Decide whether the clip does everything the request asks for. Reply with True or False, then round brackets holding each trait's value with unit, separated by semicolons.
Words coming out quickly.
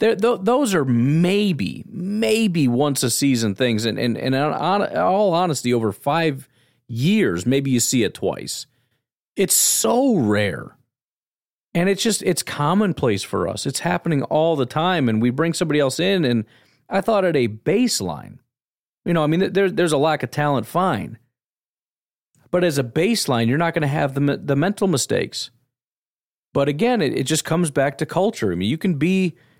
False (175 wpm)